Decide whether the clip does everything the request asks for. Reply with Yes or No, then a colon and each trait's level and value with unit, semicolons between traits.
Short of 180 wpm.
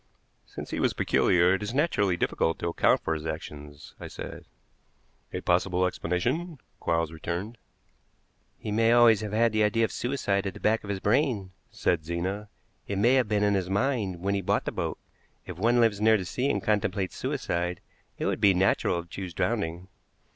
No: average, 190 wpm